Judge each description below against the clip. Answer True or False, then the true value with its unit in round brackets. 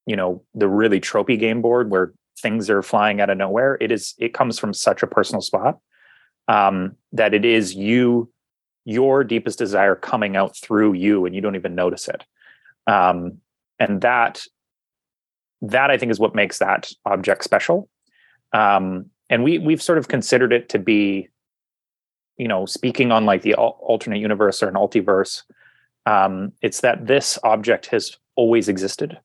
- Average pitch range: True (3.8 semitones)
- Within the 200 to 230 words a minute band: False (170 wpm)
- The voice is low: True (105 Hz)